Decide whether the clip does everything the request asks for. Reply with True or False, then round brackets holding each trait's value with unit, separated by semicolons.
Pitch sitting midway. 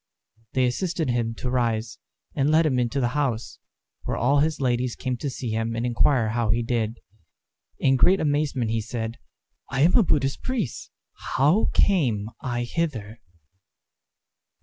False (125 Hz)